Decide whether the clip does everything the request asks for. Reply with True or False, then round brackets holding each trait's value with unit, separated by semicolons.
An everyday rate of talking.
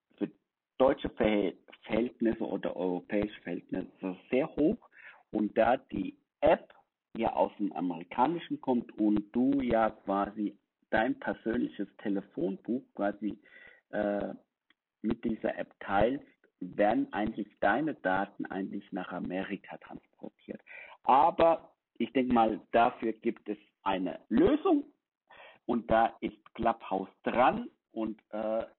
False (110 wpm)